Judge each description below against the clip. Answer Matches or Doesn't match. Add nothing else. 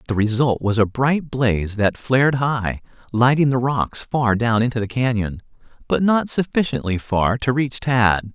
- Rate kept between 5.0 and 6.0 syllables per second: Doesn't match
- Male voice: Matches